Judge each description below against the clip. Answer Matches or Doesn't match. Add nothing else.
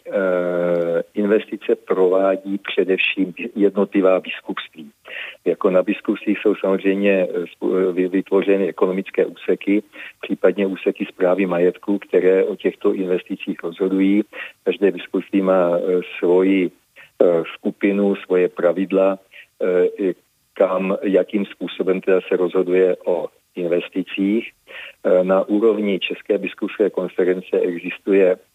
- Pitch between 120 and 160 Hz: Doesn't match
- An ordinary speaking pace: Doesn't match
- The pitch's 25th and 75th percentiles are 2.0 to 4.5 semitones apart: Doesn't match